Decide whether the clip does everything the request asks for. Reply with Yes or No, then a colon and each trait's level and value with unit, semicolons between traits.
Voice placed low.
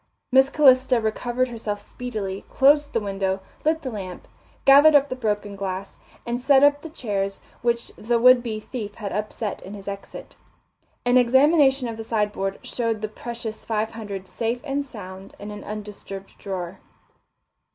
No: high, 225 Hz